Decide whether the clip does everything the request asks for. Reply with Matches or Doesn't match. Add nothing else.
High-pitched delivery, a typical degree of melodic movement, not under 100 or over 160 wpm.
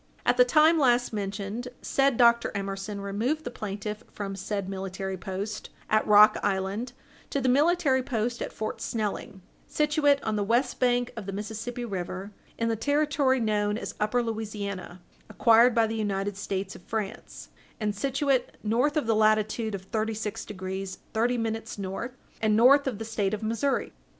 Doesn't match